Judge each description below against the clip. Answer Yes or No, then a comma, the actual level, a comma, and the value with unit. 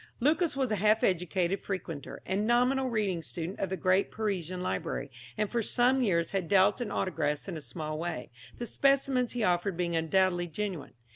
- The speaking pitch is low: No, high, 190 Hz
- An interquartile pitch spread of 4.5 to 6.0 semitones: Yes, average, 5.0 semitones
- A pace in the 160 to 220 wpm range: Yes, average, 185 wpm